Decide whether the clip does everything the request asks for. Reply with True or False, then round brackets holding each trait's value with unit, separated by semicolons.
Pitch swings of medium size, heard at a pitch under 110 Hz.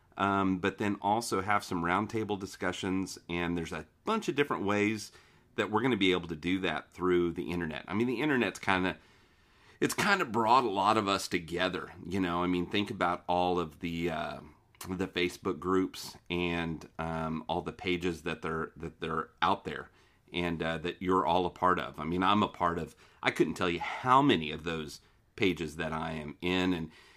False (2.1 semitones; 90 Hz)